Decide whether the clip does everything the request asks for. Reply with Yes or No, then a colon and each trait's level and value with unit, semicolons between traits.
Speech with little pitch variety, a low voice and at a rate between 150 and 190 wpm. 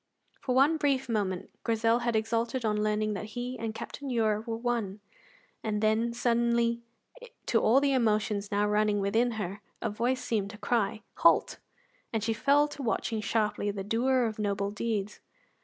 No: narrow, 2.2 semitones; high, 225 Hz; average, 170 wpm